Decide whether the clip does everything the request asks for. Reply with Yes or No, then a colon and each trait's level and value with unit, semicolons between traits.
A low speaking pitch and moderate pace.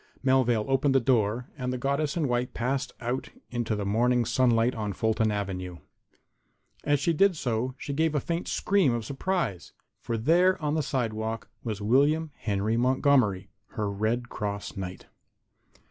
Yes: low, 125 Hz; average, 160 wpm